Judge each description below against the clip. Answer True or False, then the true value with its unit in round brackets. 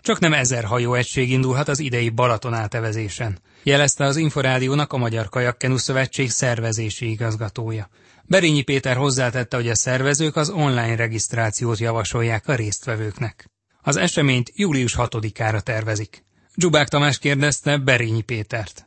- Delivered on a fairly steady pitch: False (3.7 semitones)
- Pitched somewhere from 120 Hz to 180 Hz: True (125 Hz)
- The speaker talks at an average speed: True (130 wpm)